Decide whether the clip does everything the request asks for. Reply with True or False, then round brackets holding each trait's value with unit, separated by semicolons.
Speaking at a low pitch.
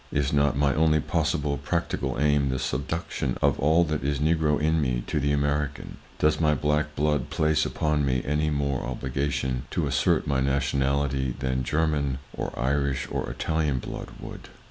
True (70 Hz)